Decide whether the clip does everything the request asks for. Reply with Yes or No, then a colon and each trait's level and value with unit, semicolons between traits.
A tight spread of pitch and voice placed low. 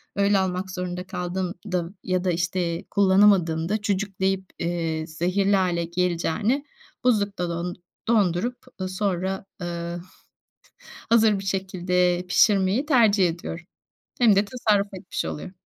No: narrow, 2.3 semitones; medium, 185 Hz